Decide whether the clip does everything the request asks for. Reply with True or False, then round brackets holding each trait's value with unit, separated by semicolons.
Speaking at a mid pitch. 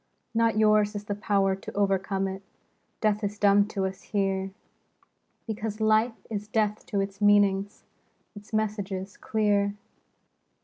False (205 Hz)